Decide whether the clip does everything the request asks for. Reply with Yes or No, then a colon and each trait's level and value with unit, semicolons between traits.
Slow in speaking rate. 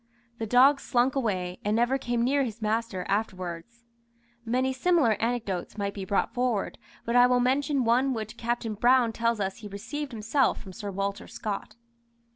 No: average, 170 wpm